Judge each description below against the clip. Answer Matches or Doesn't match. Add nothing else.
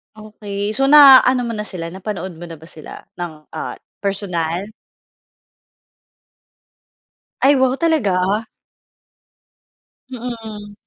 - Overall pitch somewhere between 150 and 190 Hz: Doesn't match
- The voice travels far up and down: Matches